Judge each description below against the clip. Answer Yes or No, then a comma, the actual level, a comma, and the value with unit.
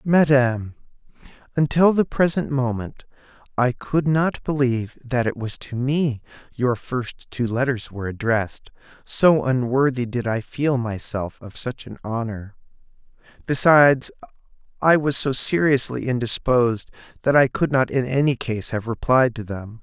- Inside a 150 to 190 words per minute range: No, average, 140 wpm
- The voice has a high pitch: No, low, 125 Hz